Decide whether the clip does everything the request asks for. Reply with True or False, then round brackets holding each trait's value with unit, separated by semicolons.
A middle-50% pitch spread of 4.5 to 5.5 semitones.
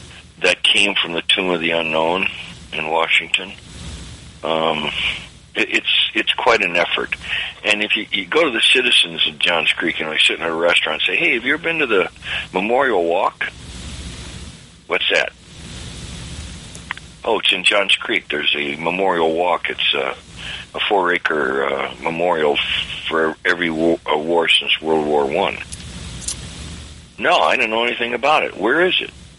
False (2.8 semitones)